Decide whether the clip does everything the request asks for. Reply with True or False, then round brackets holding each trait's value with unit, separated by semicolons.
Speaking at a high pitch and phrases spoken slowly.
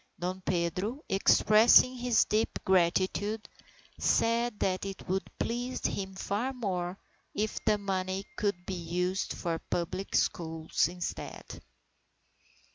True (195 Hz; 115 wpm)